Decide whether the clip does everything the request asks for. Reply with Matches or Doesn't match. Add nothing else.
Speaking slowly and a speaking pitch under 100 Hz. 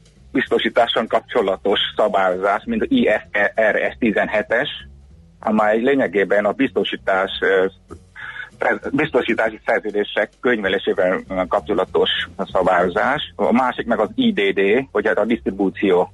Doesn't match